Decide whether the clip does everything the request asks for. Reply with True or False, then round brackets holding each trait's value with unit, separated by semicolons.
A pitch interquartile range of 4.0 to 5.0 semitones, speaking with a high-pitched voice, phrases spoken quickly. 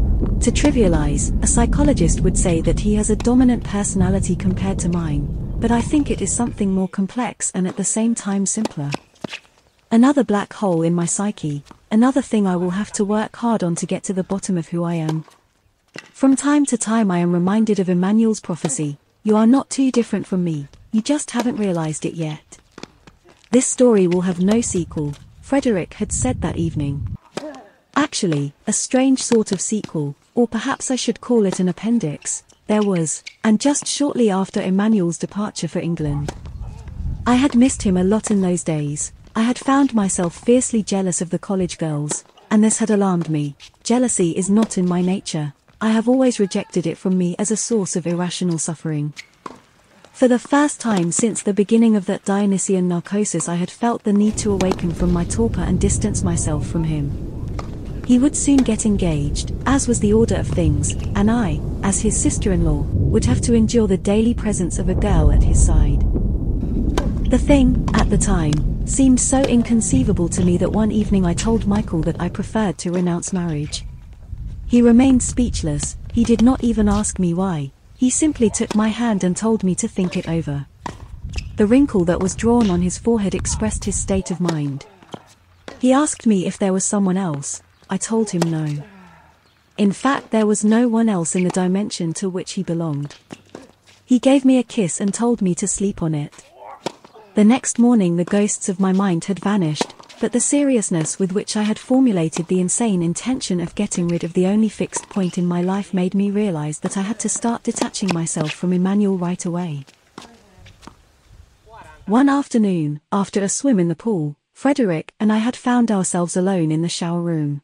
True (4.7 semitones; 195 Hz; 190 wpm)